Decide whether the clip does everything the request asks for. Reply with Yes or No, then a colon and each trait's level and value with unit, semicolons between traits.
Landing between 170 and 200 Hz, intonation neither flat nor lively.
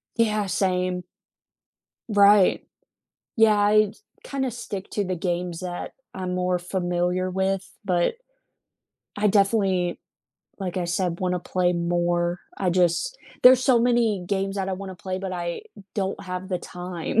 No: medium, 185 Hz; narrow, 2.3 semitones